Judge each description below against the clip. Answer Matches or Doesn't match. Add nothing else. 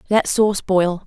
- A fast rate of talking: Doesn't match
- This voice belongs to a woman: Matches